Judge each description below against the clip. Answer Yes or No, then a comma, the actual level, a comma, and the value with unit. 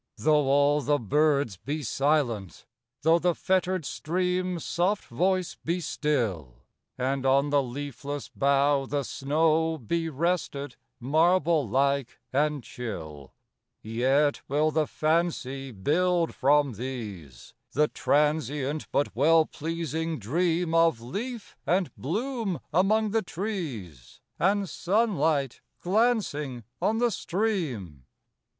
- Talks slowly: Yes, slow, 95 wpm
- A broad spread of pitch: No, average, 4.7 semitones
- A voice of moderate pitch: Yes, medium, 150 Hz